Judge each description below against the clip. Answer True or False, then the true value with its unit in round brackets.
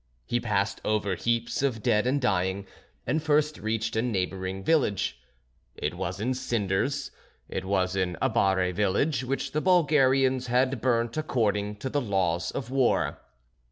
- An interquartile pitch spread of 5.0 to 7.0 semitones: True (5.3 semitones)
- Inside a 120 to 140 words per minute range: False (150 wpm)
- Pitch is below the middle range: True (115 Hz)